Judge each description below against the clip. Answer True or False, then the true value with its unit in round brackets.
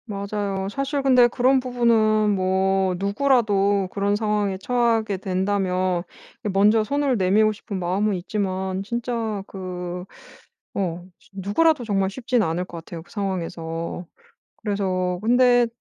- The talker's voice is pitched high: True (200 Hz)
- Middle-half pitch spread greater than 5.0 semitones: False (3.5 semitones)